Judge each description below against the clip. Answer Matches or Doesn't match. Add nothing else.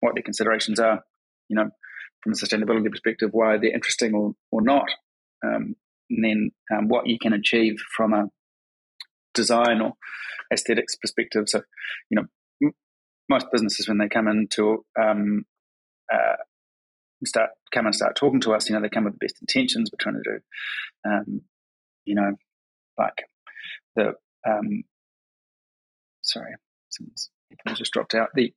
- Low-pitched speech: Matches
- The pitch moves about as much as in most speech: Doesn't match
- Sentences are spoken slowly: Doesn't match